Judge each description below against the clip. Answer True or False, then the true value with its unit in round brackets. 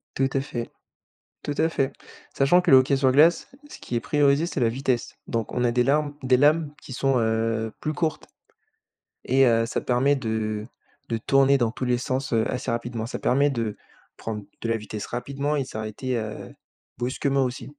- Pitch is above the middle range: False (130 Hz)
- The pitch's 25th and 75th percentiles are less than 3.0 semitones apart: False (3.4 semitones)